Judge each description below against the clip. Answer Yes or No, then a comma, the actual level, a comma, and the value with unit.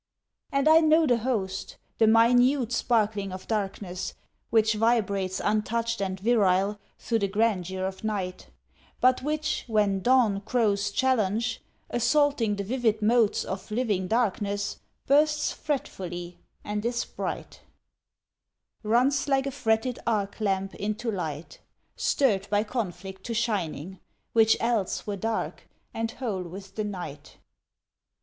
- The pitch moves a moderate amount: Yes, average, 3.6 semitones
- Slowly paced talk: Yes, slow, 130 wpm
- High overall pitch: Yes, high, 215 Hz